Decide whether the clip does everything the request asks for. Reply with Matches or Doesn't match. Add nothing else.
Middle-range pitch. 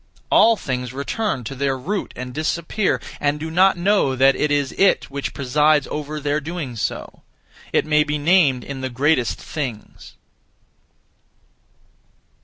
Matches